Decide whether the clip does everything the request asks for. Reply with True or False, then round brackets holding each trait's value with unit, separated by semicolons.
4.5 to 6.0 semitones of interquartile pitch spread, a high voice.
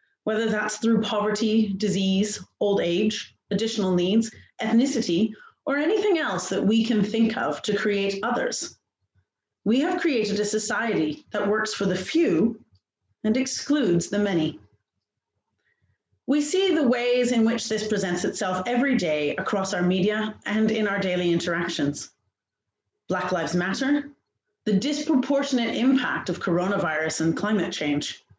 True (4.8 semitones; 210 Hz)